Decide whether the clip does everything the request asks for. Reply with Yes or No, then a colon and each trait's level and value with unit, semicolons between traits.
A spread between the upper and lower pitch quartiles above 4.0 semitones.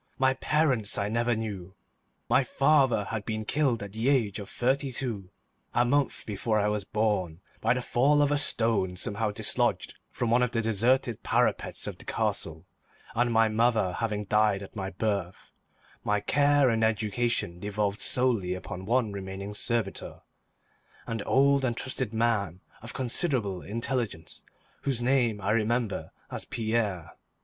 No: average, 3.5 semitones